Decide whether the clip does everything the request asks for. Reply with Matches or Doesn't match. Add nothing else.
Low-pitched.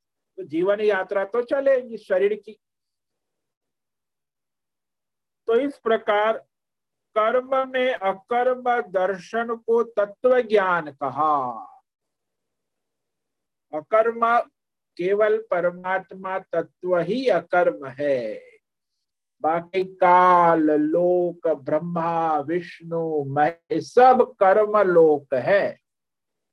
Doesn't match